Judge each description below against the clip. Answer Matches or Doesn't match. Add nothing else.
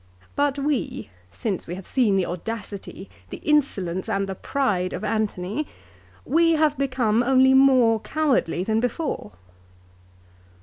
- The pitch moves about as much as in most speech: Doesn't match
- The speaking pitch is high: Matches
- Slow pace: Matches